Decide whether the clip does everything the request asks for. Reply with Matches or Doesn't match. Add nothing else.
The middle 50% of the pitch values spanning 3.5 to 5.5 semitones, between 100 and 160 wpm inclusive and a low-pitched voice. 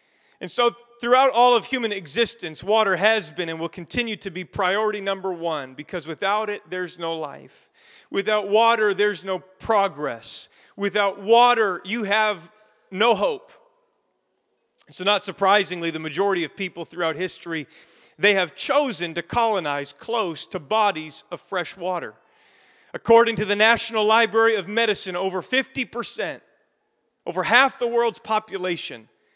Doesn't match